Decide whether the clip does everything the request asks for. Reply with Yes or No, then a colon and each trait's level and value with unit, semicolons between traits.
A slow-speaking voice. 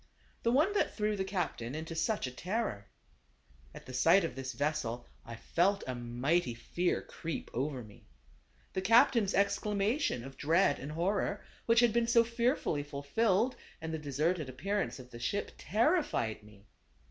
No: average, 165 wpm